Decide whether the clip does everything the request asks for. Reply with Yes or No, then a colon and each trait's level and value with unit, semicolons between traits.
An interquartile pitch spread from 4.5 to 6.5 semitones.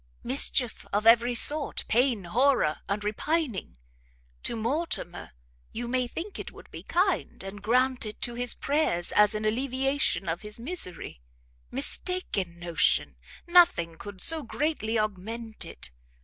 Yes: wide, 5.4 semitones